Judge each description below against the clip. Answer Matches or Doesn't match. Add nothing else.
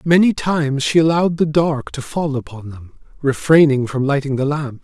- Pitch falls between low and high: Matches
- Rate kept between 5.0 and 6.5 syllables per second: Matches